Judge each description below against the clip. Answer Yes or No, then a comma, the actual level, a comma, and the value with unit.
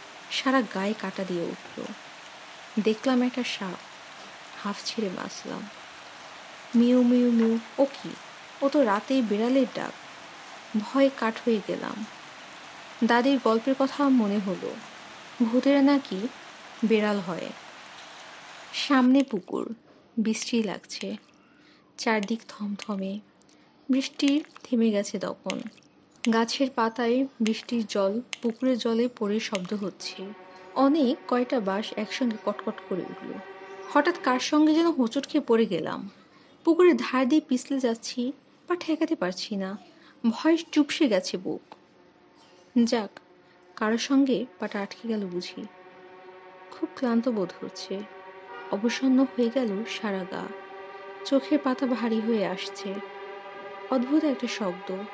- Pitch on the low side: No, high, 230 Hz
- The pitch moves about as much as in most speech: Yes, average, 4.9 semitones